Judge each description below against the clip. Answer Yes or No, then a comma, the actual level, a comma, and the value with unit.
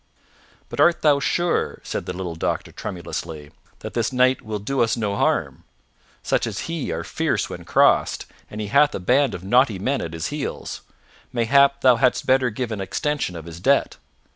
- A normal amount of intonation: No, wide, 6.8 semitones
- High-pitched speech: No, low, 120 Hz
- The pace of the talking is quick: No, average, 190 wpm